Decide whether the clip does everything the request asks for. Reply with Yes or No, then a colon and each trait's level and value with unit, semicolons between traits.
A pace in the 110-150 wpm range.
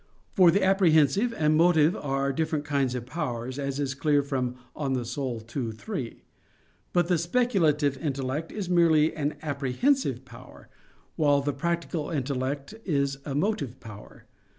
Yes: average, 145 wpm